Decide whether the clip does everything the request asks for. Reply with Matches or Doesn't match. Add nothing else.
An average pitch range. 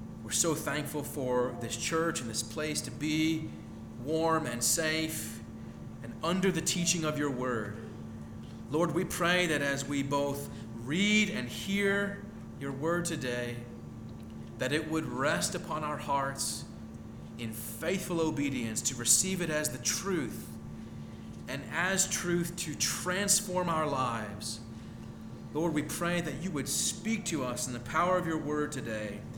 Doesn't match